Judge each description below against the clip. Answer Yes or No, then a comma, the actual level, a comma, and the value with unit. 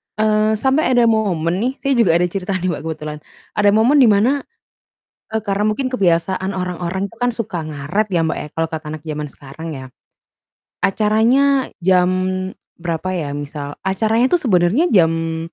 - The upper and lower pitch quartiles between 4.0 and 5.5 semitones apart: Yes, average, 5.0 semitones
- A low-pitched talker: No, high, 190 Hz